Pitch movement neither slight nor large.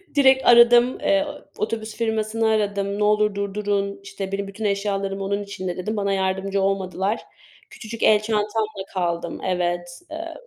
No: narrow, 2.0 semitones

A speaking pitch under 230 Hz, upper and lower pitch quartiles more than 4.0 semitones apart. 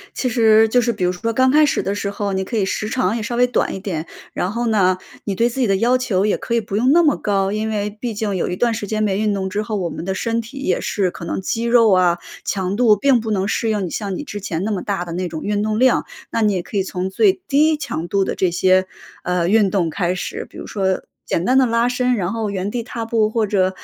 No: high, 210 Hz; average, 3.5 semitones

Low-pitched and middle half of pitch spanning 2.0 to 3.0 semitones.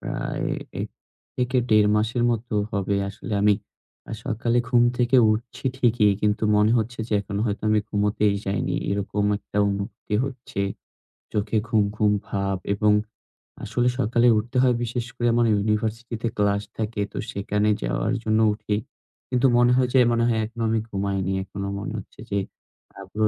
Yes: low, 110 Hz; narrow, 2.5 semitones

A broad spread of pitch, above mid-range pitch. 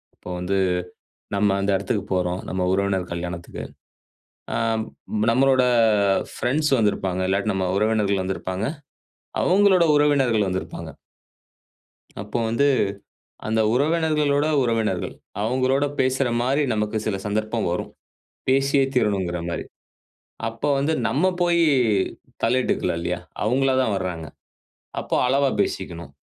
No: wide, 6.1 semitones; low, 110 Hz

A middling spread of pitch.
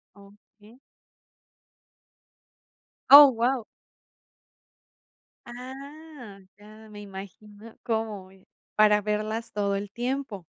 Yes: average, 3.1 semitones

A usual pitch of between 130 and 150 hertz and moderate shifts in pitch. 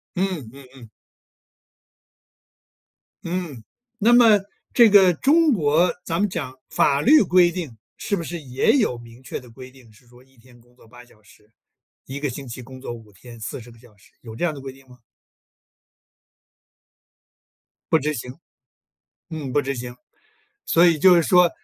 No: low, 135 Hz; wide, 6.2 semitones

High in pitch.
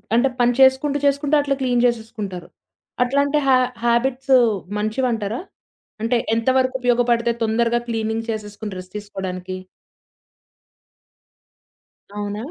Yes: high, 235 Hz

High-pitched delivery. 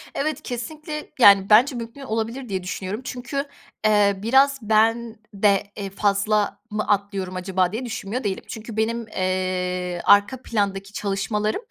Yes: high, 210 Hz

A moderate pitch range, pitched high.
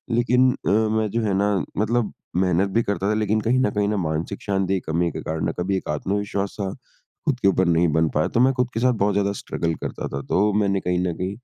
No: average, 3.2 semitones; low, 100 Hz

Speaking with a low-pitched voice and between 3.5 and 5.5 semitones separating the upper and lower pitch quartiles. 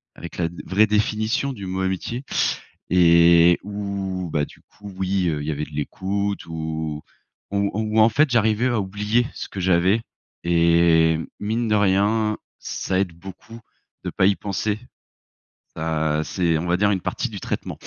Yes: very low, 95 Hz; average, 3.8 semitones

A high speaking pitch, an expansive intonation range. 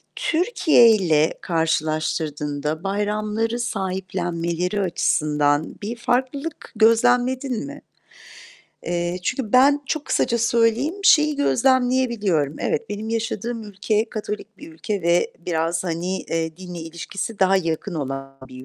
Yes: high, 200 Hz; wide, 6.1 semitones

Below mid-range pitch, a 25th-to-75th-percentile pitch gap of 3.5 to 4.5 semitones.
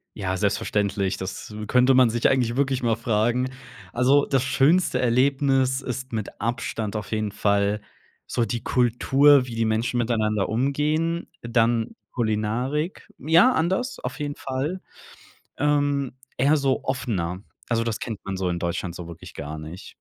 Yes: low, 120 Hz; average, 4.2 semitones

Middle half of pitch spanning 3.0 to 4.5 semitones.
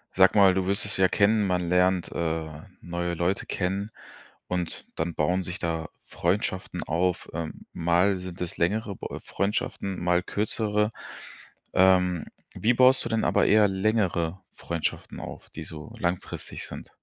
No: narrow, 2.6 semitones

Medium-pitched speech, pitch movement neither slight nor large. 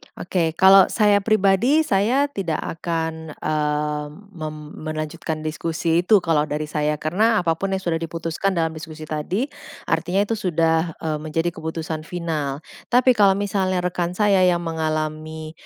Yes: medium, 165 Hz; average, 3.6 semitones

